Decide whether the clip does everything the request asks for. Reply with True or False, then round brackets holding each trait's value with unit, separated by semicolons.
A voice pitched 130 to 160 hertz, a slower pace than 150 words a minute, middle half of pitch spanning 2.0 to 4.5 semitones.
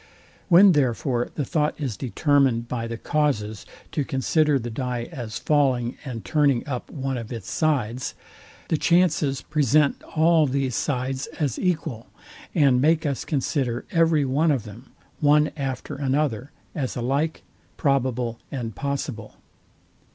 True (135 Hz; 135 wpm; 3.7 semitones)